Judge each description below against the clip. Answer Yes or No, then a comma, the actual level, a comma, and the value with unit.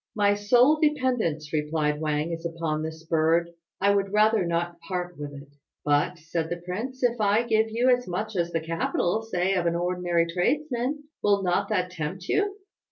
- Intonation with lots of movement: No, average, 4.7 semitones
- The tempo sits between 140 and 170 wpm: No, average, 180 wpm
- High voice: No, medium, 180 Hz